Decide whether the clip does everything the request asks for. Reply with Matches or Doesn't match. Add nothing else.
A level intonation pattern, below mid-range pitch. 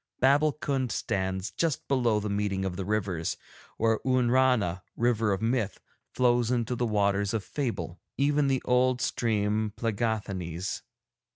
Doesn't match